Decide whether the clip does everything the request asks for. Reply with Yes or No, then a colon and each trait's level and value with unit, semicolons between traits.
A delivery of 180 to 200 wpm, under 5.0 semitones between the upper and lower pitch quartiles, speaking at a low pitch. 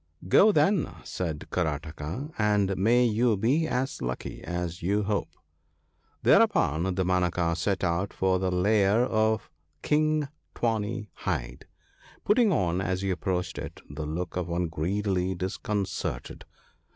No: average, 140 wpm; average, 3.9 semitones; very low, 95 Hz